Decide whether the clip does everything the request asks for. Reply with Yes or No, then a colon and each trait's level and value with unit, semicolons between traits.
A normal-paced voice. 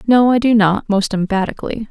Yes: average, 190 wpm